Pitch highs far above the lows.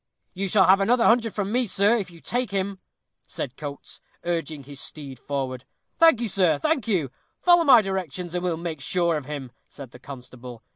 Yes: wide, 6.5 semitones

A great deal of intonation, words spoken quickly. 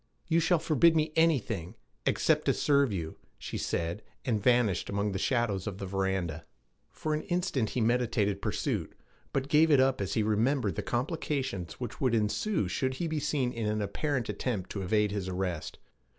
No: wide, 6.3 semitones; average, 180 wpm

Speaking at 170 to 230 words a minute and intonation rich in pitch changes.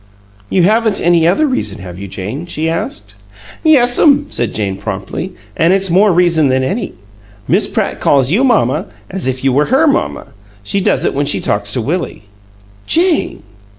Yes: average, 180 wpm; wide, 9.0 semitones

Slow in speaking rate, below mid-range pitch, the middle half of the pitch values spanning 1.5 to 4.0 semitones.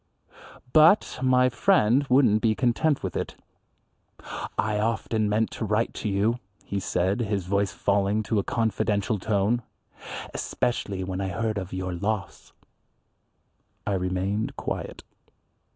Yes: slow, 130 wpm; low, 105 Hz; average, 2.9 semitones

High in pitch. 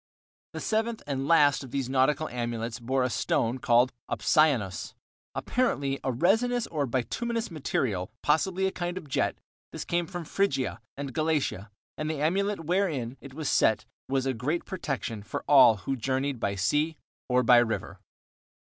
No: medium, 140 Hz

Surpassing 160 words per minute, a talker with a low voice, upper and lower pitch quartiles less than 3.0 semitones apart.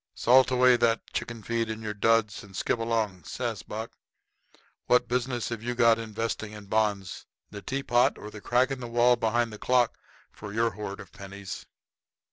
Yes: average, 185 wpm; low, 115 Hz; narrow, 2.4 semitones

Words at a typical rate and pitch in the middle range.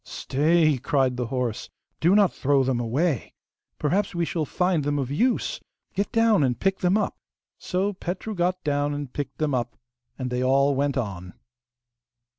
Yes: average, 170 wpm; medium, 145 Hz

